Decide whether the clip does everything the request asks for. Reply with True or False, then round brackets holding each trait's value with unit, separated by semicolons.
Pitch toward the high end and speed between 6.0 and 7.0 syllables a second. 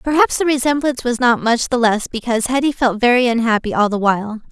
True (240 Hz; 6.2 syllables/s)